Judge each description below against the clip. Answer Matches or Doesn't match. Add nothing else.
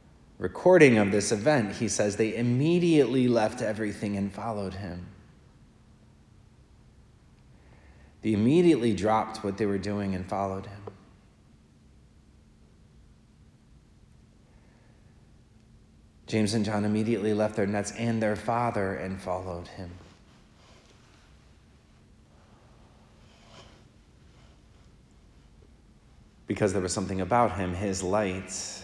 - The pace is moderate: Doesn't match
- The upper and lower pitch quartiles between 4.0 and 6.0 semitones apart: Doesn't match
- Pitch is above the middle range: Doesn't match